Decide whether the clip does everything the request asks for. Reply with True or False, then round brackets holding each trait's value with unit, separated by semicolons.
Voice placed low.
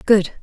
False (200 Hz)